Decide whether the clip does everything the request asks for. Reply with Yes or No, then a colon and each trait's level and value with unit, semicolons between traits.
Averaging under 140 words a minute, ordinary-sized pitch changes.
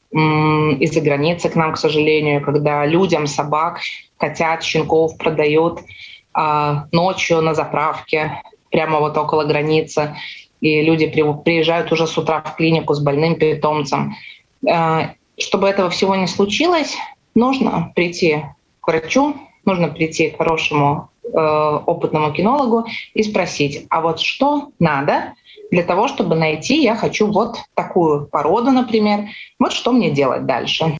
Yes: average, 130 wpm; average, 4.0 semitones